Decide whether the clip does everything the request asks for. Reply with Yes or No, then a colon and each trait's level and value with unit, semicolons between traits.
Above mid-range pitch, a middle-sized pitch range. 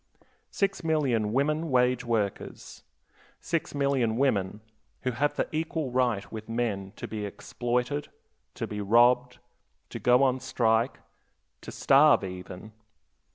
No: low, 125 Hz; average, 4.0 semitones